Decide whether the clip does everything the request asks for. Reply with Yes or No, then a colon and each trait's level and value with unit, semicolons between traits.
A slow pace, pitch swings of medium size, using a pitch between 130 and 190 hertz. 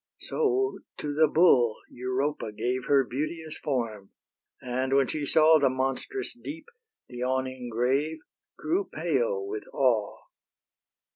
Yes: slow, 125 wpm; average, 4.4 semitones; medium, 140 Hz